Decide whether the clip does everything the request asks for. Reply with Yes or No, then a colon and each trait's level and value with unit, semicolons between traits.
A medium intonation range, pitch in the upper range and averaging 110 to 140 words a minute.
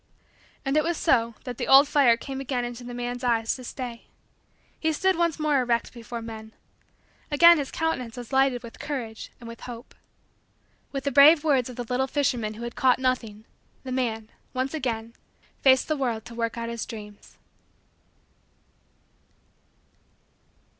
No: average, 3.0 semitones; very high, 250 Hz; average, 165 wpm